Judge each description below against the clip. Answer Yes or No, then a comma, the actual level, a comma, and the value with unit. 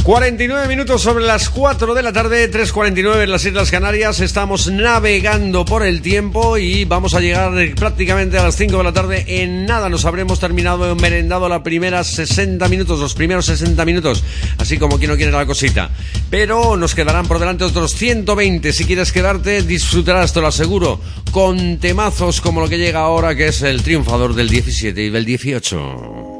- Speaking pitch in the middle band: No, low, 120 Hz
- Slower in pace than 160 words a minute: No, average, 185 wpm